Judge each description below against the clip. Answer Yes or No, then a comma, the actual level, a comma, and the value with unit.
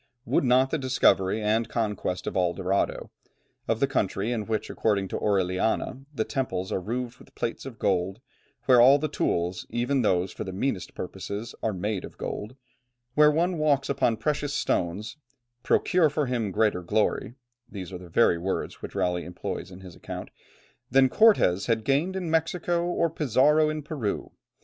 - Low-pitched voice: Yes, low, 115 Hz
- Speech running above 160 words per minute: Yes, average, 175 wpm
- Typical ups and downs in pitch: No, wide, 6.5 semitones